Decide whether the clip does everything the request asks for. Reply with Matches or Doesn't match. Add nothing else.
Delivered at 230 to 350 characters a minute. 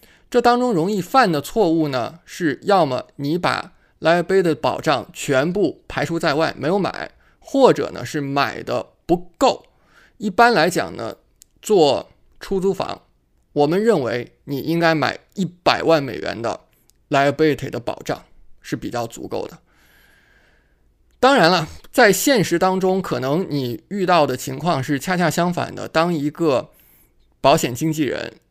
Matches